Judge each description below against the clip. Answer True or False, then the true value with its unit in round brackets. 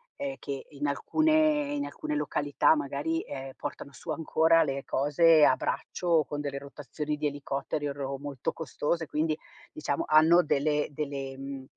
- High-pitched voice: False (145 Hz)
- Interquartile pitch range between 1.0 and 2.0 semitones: False (2.6 semitones)